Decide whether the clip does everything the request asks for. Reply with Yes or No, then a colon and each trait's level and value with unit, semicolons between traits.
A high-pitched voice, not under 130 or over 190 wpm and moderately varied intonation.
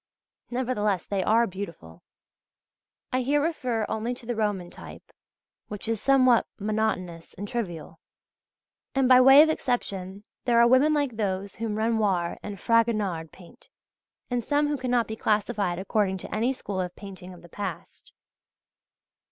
Yes: high, 215 Hz; average, 150 wpm; average, 4.4 semitones